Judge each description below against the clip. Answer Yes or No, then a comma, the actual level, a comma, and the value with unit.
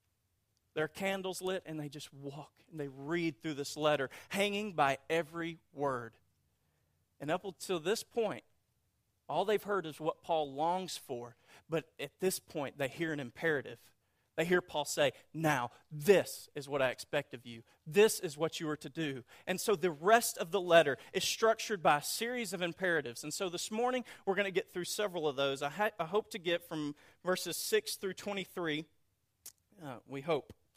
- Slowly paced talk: No, average, 190 wpm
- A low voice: No, medium, 160 Hz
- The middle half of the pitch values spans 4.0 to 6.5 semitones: Yes, average, 5.2 semitones